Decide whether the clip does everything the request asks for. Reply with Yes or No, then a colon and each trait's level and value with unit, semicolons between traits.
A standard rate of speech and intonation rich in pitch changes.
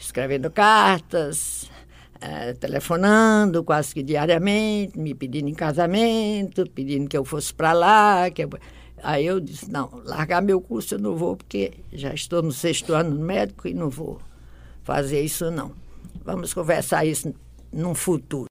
No: average, 155 wpm; average, 4.5 semitones